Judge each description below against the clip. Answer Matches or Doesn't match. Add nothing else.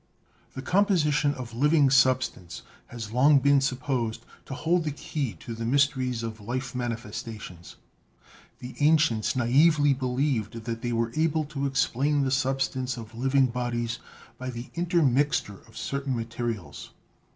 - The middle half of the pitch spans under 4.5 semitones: Matches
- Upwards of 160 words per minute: Doesn't match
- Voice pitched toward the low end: Matches